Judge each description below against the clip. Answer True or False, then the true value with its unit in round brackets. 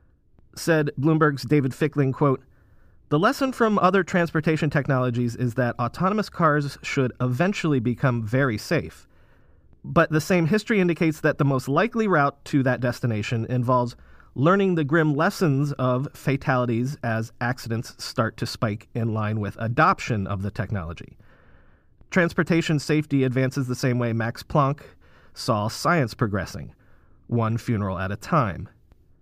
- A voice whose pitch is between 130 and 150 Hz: True (135 Hz)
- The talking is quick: False (140 wpm)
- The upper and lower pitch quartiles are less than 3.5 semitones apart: False (5.1 semitones)